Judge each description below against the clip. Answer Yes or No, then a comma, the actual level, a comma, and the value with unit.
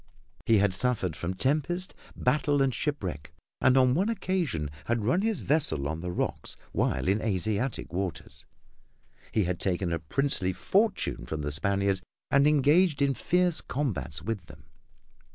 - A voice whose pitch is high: No, low, 115 Hz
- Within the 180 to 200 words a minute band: No, average, 155 wpm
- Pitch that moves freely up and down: Yes, wide, 8.4 semitones